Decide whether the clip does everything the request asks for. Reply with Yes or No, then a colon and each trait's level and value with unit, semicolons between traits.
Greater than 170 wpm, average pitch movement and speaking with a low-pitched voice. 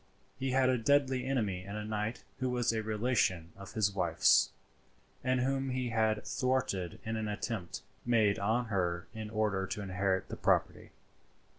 No: average, 165 wpm; average, 4.2 semitones; low, 110 Hz